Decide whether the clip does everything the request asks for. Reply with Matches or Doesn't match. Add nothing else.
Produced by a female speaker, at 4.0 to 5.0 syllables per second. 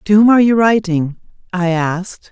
Doesn't match